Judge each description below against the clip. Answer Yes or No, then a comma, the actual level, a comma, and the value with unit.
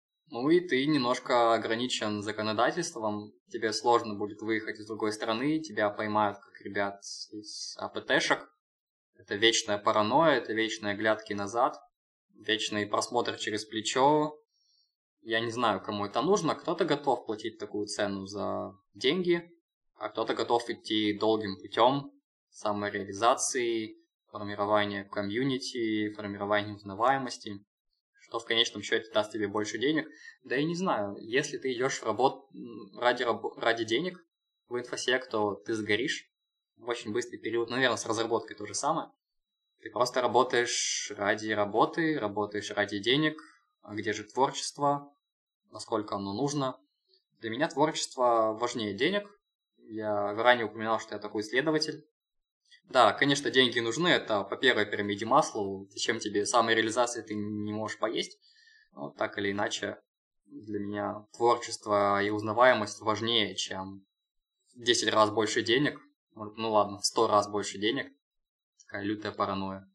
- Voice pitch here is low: Yes, low, 110 Hz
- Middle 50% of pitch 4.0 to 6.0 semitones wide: Yes, average, 4.6 semitones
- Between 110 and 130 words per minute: No, average, 140 wpm